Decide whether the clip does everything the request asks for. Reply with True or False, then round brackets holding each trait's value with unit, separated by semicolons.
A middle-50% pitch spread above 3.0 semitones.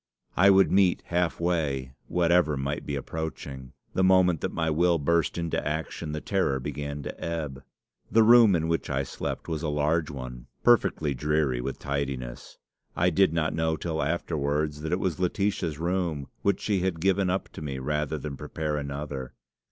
True (3.6 semitones)